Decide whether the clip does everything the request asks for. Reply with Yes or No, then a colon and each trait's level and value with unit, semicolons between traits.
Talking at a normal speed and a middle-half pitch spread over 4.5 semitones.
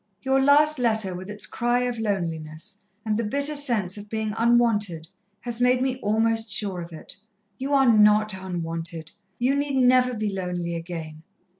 Yes: average, 165 wpm; wide, 5.6 semitones